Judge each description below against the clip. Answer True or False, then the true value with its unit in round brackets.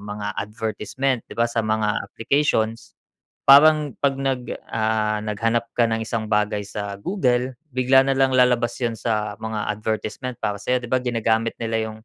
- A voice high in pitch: False (115 Hz)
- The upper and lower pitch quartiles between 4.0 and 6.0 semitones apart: False (2.9 semitones)